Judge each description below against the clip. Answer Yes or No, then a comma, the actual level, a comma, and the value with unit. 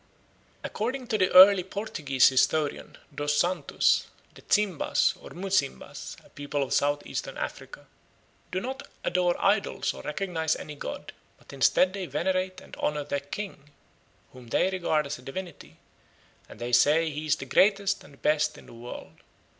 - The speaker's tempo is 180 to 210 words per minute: No, average, 160 wpm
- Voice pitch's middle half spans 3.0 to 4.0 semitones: No, average, 4.9 semitones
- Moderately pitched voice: Yes, medium, 160 Hz